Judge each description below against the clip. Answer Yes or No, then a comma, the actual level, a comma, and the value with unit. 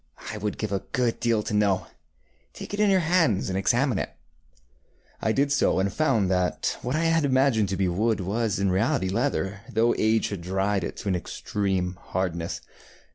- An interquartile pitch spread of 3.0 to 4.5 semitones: No, average, 5.2 semitones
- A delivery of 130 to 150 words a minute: No, average, 190 wpm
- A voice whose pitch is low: Yes, low, 105 Hz